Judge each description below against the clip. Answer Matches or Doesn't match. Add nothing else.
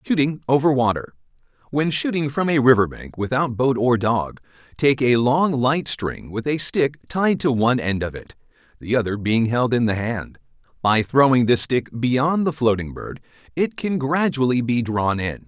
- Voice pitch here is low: Matches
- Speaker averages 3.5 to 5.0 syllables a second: Matches